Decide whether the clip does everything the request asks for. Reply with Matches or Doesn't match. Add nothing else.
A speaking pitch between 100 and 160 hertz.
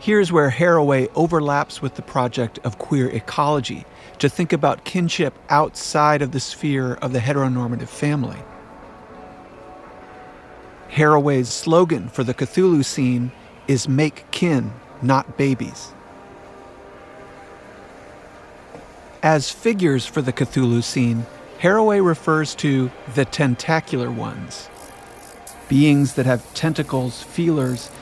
Matches